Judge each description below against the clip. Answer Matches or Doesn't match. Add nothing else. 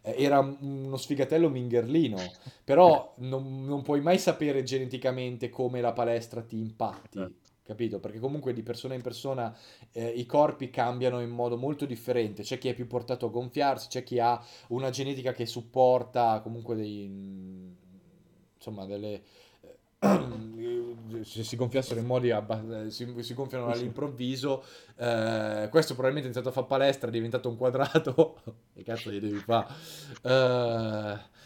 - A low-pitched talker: Matches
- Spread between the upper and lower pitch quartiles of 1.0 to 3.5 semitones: Matches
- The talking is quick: Doesn't match